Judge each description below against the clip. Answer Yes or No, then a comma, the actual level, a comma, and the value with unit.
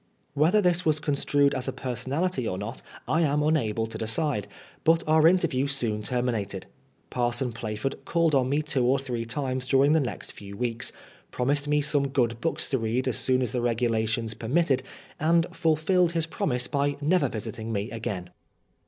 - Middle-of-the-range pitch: No, low, 130 Hz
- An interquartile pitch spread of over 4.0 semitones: Yes, average, 4.7 semitones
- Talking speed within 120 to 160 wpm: No, average, 180 wpm